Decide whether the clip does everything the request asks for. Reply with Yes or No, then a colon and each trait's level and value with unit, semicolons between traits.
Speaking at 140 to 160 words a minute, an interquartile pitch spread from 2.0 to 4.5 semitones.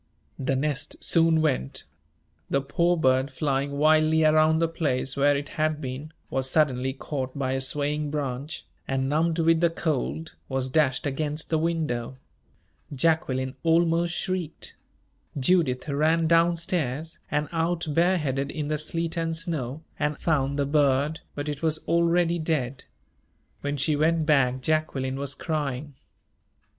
Yes: average, 145 wpm; average, 3.2 semitones